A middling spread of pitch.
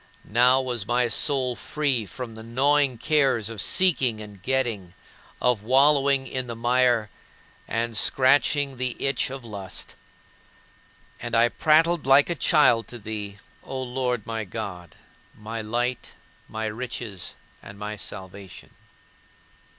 Yes: average, 3.5 semitones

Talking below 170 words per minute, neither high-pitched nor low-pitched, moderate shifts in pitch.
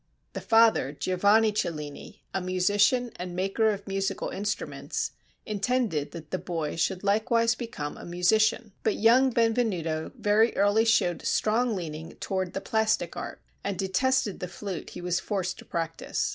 No: average, 150 wpm; high, 200 Hz; average, 3.8 semitones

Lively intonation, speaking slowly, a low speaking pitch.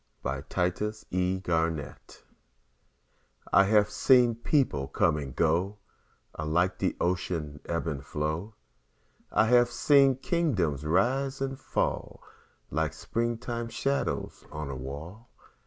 Yes: wide, 7.4 semitones; slow, 115 wpm; very low, 95 Hz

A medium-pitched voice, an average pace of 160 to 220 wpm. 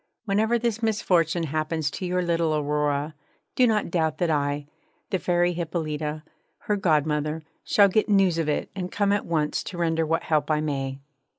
Yes: medium, 165 Hz; average, 175 wpm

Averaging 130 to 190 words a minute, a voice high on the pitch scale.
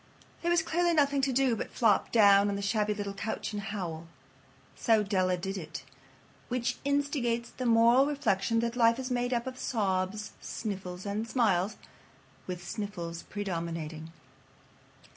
Yes: average, 150 wpm; high, 215 Hz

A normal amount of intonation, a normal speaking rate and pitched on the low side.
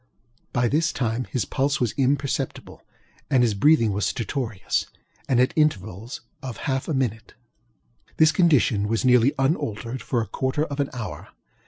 Yes: average, 3.7 semitones; average, 155 wpm; low, 130 Hz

